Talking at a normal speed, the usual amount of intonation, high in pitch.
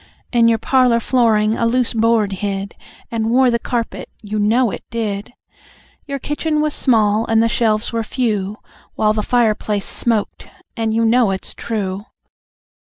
No: average, 160 wpm; narrow, 2.2 semitones; high, 225 Hz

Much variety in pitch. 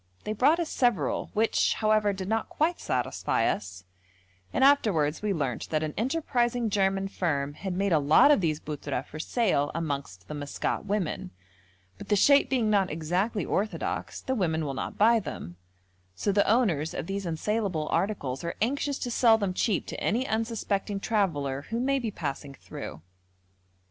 Yes: wide, 6.6 semitones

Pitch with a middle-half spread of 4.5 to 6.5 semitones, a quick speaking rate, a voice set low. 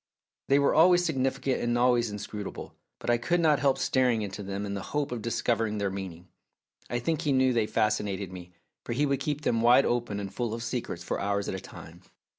Yes: average, 4.8 semitones; fast, 225 wpm; low, 120 Hz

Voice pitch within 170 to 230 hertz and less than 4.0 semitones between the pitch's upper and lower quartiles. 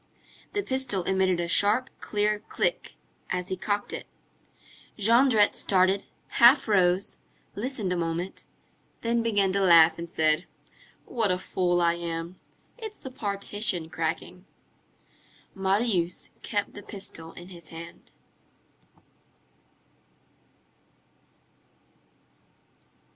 Yes: high, 190 Hz; average, 3.5 semitones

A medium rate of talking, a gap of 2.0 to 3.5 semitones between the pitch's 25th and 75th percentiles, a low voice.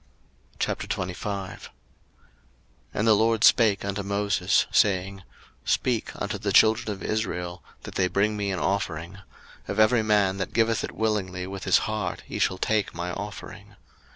Yes: average, 155 wpm; narrow, 2.4 semitones; low, 100 Hz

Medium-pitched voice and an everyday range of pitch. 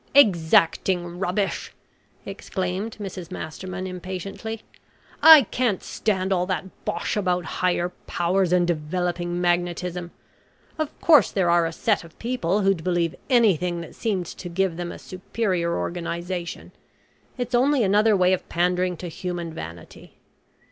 No: medium, 180 Hz; narrow, 2.3 semitones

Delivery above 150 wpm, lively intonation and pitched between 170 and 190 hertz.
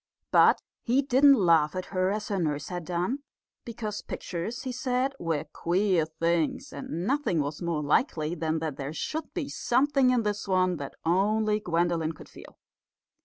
Yes: average, 170 wpm; wide, 6.6 semitones; medium, 185 Hz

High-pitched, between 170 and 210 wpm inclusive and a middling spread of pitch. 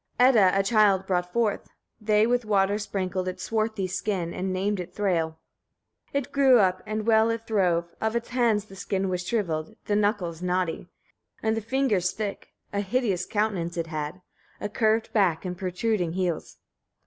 Yes: high, 200 Hz; average, 175 wpm; average, 3.3 semitones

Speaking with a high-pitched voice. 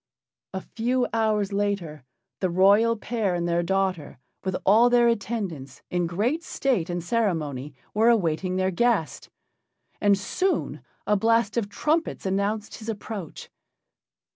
Yes: high, 200 Hz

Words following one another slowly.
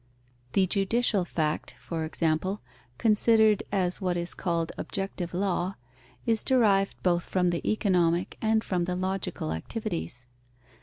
Yes: slow, 130 wpm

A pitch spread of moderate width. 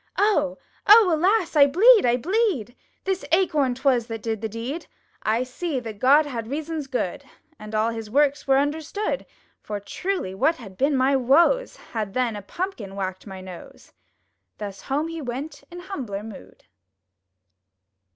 No: wide, 6.7 semitones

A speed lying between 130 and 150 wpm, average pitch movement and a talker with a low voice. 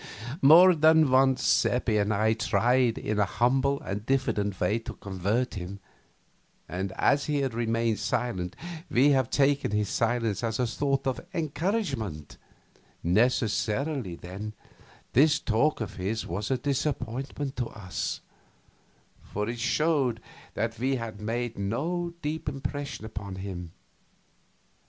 Yes: slow, 135 wpm; average, 4.8 semitones; low, 120 Hz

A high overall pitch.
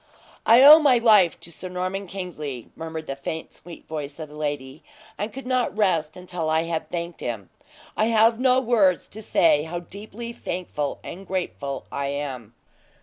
No: medium, 175 Hz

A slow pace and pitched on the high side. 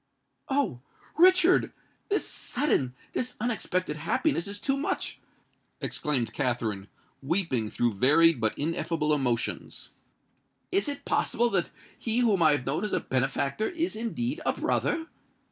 No: slow, 125 wpm; medium, 170 Hz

